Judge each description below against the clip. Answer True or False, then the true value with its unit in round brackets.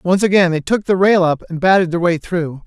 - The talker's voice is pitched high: False (180 Hz)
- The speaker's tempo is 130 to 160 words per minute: False (270 wpm)